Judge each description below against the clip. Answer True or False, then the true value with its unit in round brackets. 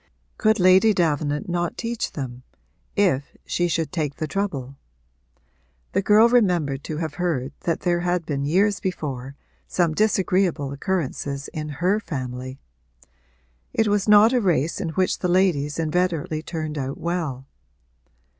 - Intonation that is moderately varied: True (4.7 semitones)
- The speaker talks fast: False (140 wpm)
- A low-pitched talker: False (170 Hz)